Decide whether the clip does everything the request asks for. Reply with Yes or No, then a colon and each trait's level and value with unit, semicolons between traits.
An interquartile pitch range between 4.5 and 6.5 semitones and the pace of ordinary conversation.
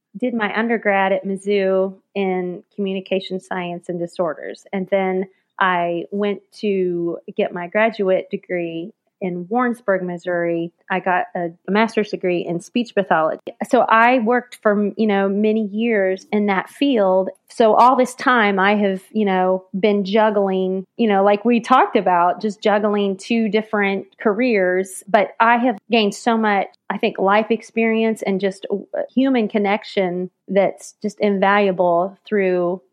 No: average, 2.7 semitones; average, 145 wpm